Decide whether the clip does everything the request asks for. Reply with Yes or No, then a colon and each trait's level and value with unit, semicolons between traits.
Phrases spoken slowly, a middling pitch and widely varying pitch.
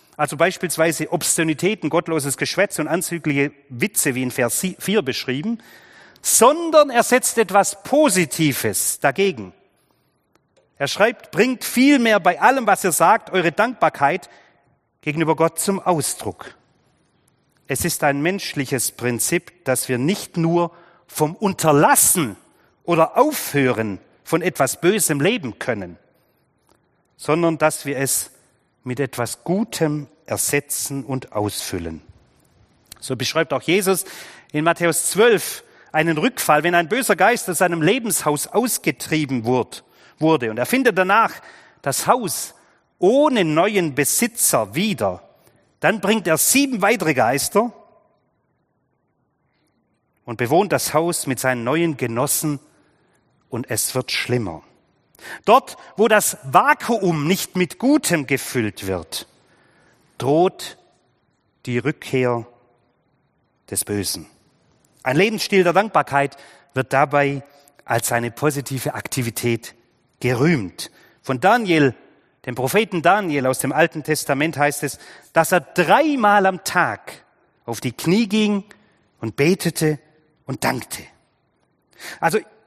Yes: slow, 115 wpm; medium, 155 Hz; wide, 6.0 semitones